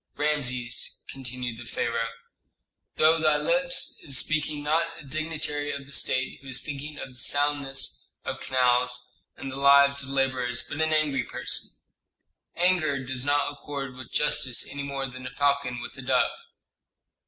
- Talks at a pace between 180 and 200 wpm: No, average, 160 wpm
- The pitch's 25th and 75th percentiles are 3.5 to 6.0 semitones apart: No, average, 2.7 semitones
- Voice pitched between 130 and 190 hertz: Yes, medium, 140 Hz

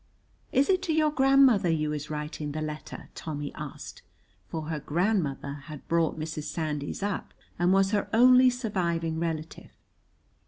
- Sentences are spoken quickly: No, average, 150 wpm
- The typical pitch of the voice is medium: Yes, medium, 165 Hz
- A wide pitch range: Yes, wide, 6.5 semitones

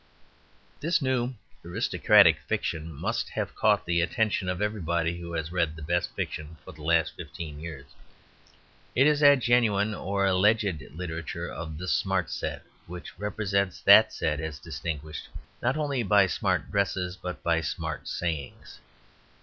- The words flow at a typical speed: Yes, average, 150 wpm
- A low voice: Yes, very low, 90 Hz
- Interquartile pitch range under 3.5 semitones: No, average, 4.2 semitones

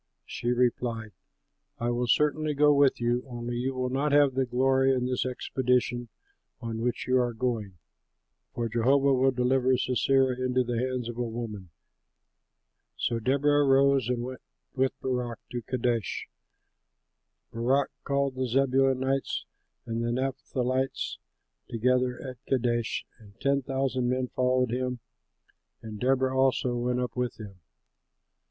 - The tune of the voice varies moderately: No, narrow, 1.8 semitones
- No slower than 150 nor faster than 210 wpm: No, average, 140 wpm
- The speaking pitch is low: Yes, low, 125 Hz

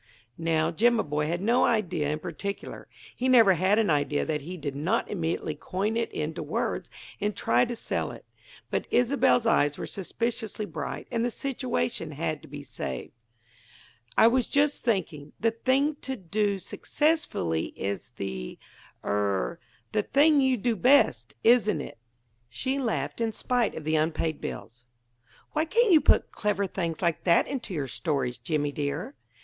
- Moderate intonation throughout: No, wide, 8.0 semitones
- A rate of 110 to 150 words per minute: No, average, 160 wpm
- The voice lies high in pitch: Yes, high, 195 Hz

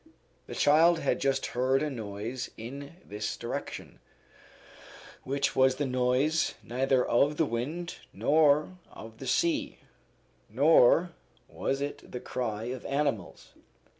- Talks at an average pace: No, slow, 125 wpm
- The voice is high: No, low, 135 Hz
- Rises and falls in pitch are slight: No, average, 3.4 semitones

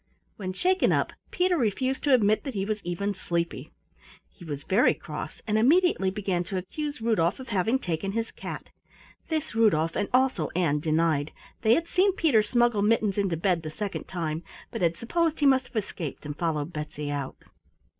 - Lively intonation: Yes, wide, 6.5 semitones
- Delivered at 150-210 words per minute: Yes, average, 185 wpm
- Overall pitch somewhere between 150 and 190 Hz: No, high, 200 Hz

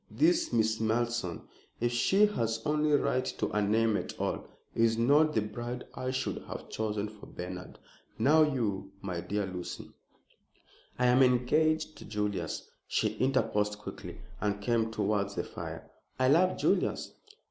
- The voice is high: No, low, 115 Hz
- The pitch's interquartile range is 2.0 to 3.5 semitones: No, average, 4.1 semitones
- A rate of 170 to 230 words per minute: No, average, 155 wpm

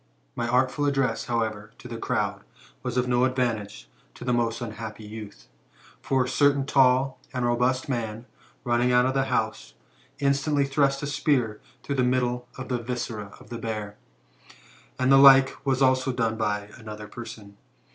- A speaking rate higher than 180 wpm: No, average, 170 wpm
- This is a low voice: Yes, low, 125 Hz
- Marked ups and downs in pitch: No, average, 3.0 semitones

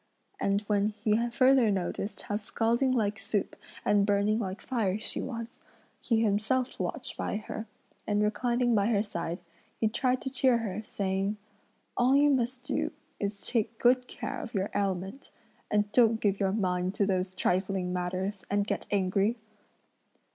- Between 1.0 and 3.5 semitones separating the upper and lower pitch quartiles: Yes, average, 3.0 semitones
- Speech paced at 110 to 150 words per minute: No, average, 160 wpm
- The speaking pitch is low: No, high, 210 Hz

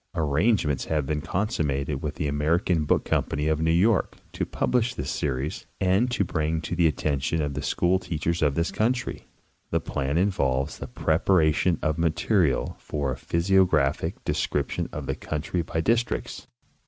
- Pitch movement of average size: Yes, average, 3.8 semitones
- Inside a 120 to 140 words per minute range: No, average, 170 wpm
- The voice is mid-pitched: No, very low, 80 Hz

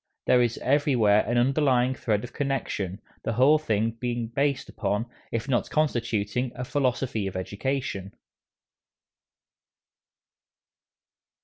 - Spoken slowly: Yes, slow, 105 wpm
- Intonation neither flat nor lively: Yes, average, 3.9 semitones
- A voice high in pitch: No, low, 120 Hz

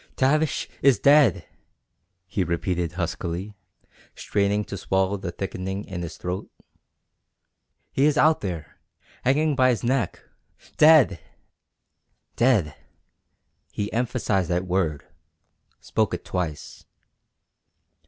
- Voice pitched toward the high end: No, low, 100 Hz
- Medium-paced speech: No, slow, 105 wpm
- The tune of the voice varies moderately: No, wide, 6.4 semitones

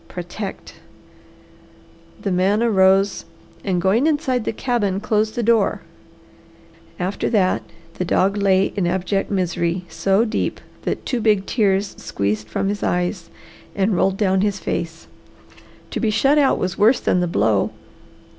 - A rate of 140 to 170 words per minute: Yes, average, 145 wpm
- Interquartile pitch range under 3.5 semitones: Yes, average, 2.9 semitones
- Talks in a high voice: Yes, high, 195 Hz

